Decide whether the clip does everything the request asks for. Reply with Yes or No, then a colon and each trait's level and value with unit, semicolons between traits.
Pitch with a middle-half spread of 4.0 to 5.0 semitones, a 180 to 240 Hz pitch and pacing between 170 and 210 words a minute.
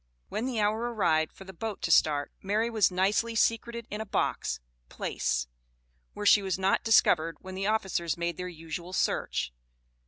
Yes: average, 4.3 semitones; high, 190 Hz; average, 175 wpm